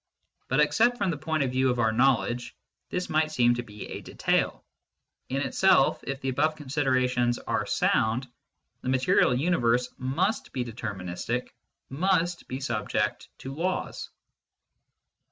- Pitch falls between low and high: No, low, 130 Hz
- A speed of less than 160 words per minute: Yes, average, 140 wpm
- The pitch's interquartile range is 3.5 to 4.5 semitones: Yes, average, 4.2 semitones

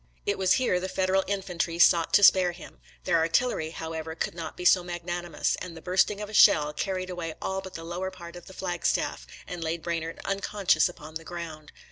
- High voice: No, medium, 175 Hz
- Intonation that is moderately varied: No, narrow, 2.3 semitones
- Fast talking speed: Yes, fast, 210 wpm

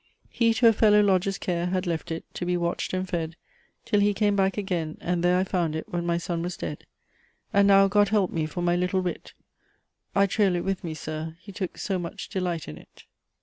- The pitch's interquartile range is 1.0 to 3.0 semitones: Yes, narrow, 2.5 semitones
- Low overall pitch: No, medium, 180 Hz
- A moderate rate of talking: No, fast, 230 wpm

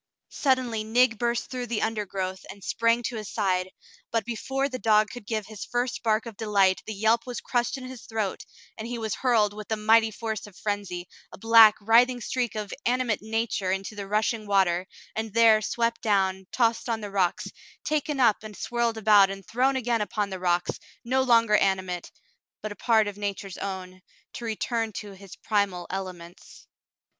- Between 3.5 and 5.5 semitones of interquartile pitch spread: No, average, 2.9 semitones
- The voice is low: No, high, 215 Hz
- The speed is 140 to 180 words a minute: No, average, 190 wpm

